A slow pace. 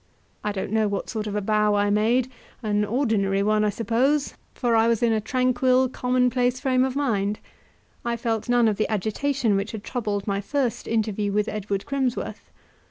No: average, 185 wpm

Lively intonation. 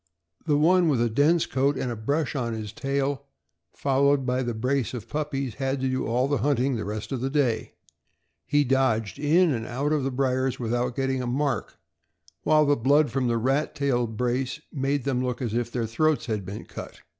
No: average, 2.9 semitones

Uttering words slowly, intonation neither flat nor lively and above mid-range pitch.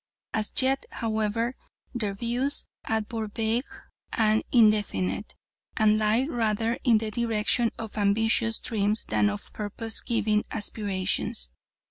No: slow, 120 wpm; narrow, 1.7 semitones; high, 220 Hz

